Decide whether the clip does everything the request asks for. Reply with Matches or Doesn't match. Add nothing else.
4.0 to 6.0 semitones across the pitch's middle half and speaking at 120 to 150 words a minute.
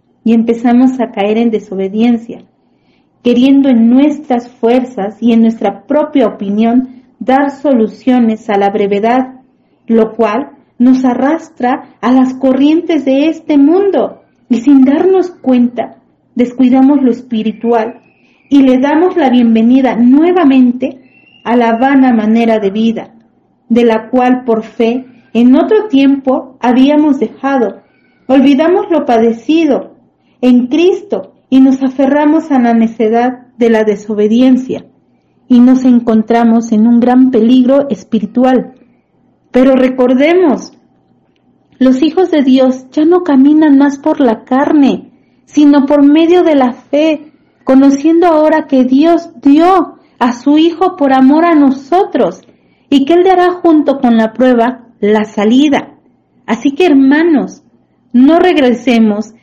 Doesn't match